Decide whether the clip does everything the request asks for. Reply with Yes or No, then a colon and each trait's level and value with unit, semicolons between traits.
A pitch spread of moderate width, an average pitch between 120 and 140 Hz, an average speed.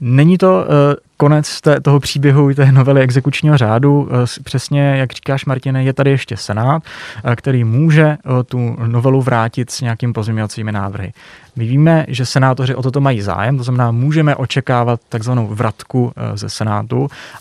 Yes: average, 3.0 semitones; low, 130 Hz; average, 150 wpm